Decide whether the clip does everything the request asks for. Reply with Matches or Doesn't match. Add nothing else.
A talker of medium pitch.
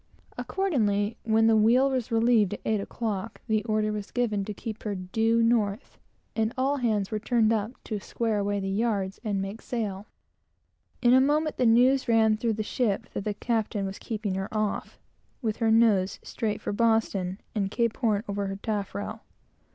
Doesn't match